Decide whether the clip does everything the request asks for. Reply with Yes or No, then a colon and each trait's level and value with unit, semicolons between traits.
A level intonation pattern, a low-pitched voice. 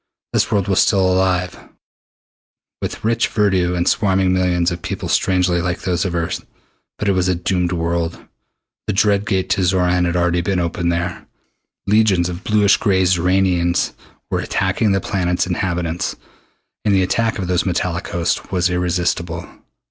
Yes: narrow, 1.6 semitones; very low, 90 Hz